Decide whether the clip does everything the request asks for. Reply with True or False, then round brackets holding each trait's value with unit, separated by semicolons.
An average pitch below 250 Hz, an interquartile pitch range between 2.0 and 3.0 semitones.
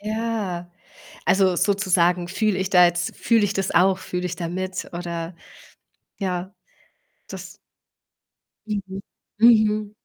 True (190 Hz; 2.7 semitones)